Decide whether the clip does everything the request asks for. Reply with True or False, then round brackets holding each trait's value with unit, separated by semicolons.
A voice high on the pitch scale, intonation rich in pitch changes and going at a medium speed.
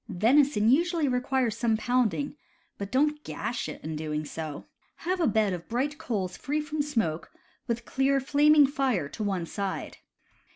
True (245 Hz; 6.4 semitones; 165 wpm)